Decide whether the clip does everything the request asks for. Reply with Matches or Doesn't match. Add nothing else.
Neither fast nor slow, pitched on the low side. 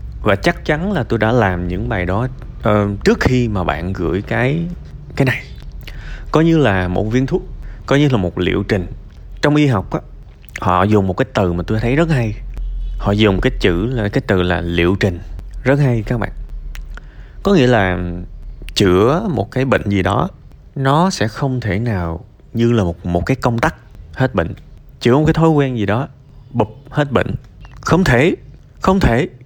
Matches